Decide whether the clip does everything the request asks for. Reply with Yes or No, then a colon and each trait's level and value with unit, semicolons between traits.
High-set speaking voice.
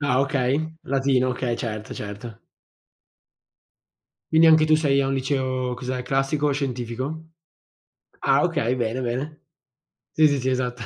No: low, 130 Hz